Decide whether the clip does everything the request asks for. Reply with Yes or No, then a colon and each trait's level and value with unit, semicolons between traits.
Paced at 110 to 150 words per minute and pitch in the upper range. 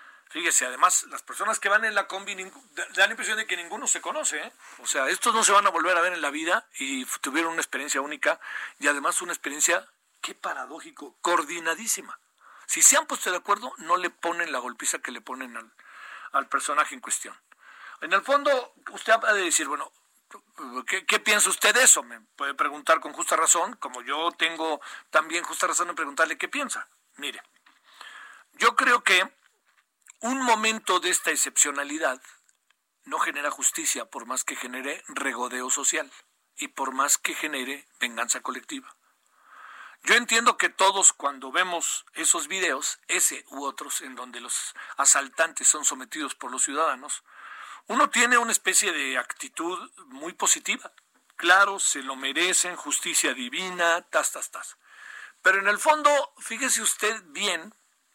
No: average, 165 wpm; high, 195 Hz